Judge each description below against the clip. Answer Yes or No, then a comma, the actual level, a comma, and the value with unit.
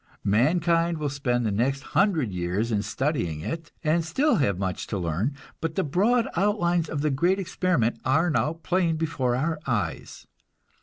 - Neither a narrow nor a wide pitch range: No, wide, 6.6 semitones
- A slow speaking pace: No, average, 165 wpm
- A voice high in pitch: No, medium, 150 Hz